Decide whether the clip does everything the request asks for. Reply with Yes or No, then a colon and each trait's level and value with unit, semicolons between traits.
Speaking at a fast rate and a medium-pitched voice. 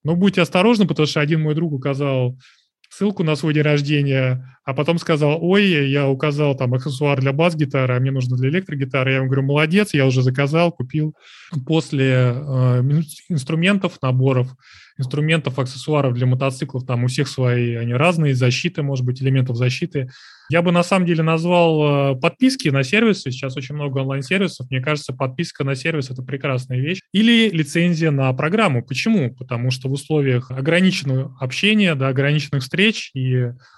Yes: fast, 165 wpm; medium, 145 Hz